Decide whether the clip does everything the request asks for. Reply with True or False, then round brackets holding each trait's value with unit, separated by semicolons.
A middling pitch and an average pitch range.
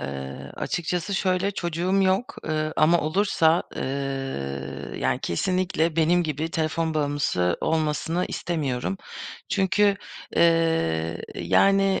True (160 Hz; 4.6 semitones)